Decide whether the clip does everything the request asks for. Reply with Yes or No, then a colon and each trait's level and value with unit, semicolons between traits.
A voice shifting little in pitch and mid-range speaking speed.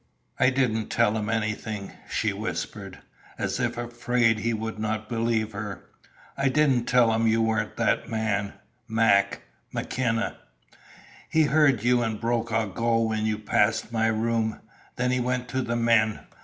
Yes: narrow, 1.7 semitones; average, 155 wpm